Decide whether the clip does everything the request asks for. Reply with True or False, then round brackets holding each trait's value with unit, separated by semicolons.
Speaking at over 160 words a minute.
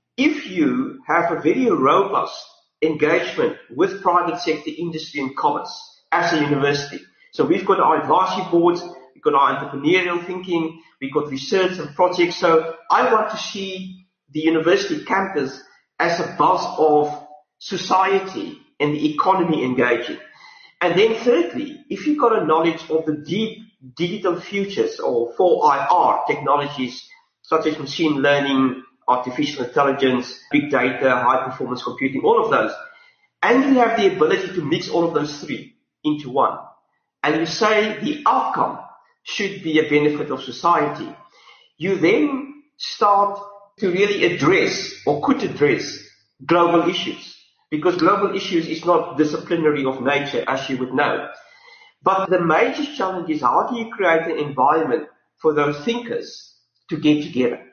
False (150 wpm)